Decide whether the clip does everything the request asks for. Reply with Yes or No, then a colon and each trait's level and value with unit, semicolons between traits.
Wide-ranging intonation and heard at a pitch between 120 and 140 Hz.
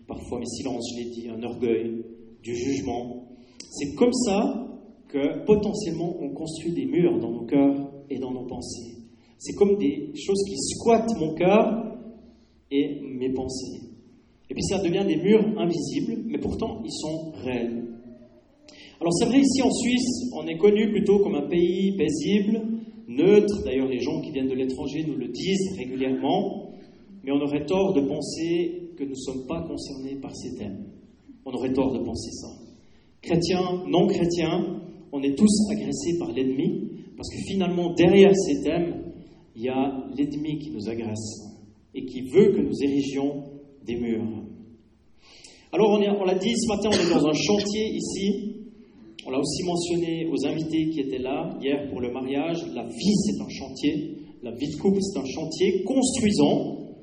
No: wide, 7.3 semitones; medium, 155 Hz